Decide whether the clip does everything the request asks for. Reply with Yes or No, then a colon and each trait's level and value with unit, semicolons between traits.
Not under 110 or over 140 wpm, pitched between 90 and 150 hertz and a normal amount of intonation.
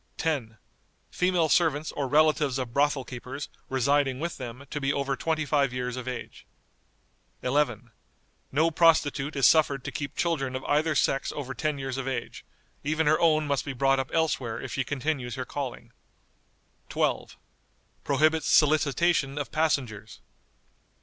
No: average, 150 wpm; medium, 140 Hz; average, 3.0 semitones